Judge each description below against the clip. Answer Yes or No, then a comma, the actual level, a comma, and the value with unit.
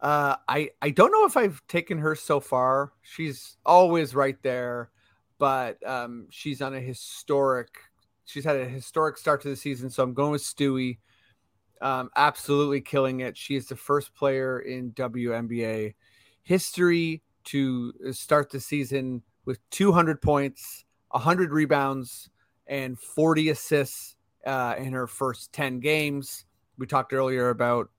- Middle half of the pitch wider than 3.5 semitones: No, average, 3.0 semitones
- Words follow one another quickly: No, average, 145 wpm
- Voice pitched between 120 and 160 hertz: Yes, low, 135 Hz